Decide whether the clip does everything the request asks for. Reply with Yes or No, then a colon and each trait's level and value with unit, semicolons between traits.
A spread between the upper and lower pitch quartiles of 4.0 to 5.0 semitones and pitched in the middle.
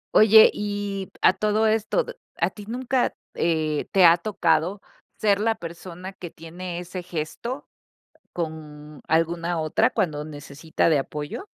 Yes: average, 4.7 semitones; medium, 175 Hz